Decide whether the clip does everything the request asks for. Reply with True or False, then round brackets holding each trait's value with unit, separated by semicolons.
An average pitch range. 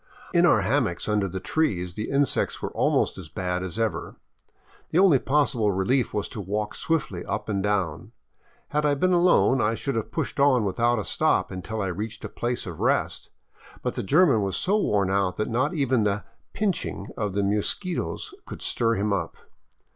False (6.1 semitones)